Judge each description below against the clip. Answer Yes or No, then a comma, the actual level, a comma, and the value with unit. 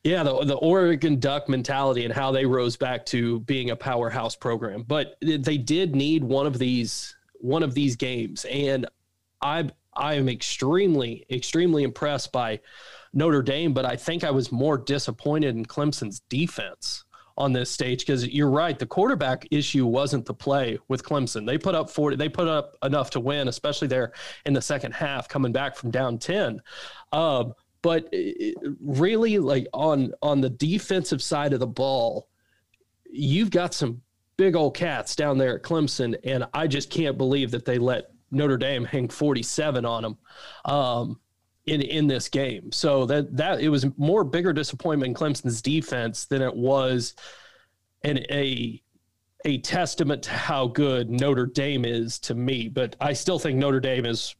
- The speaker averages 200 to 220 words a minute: No, average, 170 wpm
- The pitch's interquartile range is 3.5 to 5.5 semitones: No, average, 3.1 semitones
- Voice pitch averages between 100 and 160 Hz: Yes, medium, 140 Hz